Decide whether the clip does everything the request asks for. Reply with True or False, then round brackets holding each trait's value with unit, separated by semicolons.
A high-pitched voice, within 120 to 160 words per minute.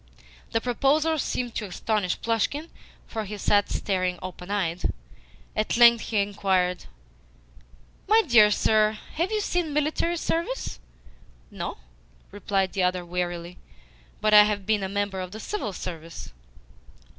True (210 Hz; 135 wpm)